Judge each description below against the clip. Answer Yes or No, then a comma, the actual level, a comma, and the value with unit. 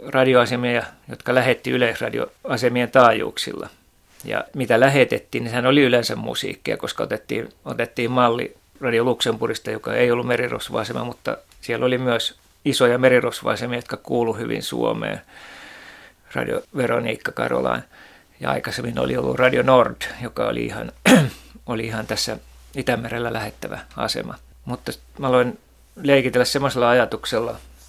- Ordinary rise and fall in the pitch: No, narrow, 1.6 semitones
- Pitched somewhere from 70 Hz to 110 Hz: No, low, 120 Hz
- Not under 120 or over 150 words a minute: Yes, average, 125 wpm